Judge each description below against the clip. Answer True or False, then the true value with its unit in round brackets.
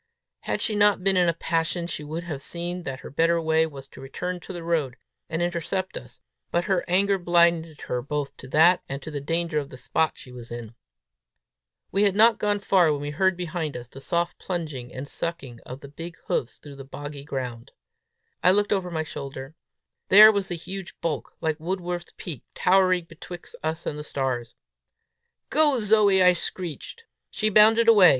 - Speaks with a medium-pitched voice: True (170 Hz)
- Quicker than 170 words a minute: True (195 wpm)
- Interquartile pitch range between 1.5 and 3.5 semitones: False (4.3 semitones)